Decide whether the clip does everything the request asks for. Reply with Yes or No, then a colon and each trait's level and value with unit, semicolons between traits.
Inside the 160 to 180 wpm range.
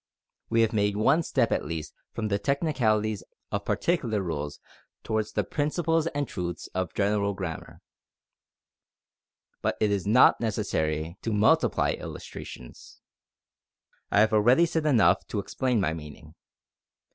No: slow, 135 wpm